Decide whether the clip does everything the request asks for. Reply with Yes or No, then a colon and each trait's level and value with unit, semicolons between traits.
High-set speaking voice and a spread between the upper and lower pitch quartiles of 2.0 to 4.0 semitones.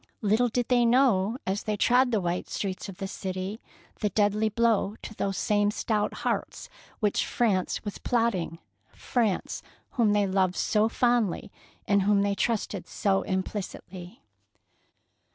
Yes: high, 205 Hz; average, 2.9 semitones